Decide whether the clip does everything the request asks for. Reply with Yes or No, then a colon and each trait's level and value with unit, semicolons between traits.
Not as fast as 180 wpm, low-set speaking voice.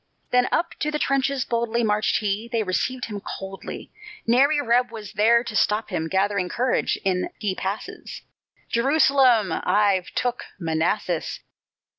No: average, 140 wpm; high, 225 Hz